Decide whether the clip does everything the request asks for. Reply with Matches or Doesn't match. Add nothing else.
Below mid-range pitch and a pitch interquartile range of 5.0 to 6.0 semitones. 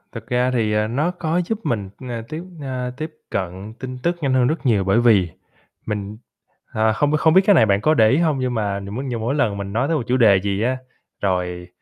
Matches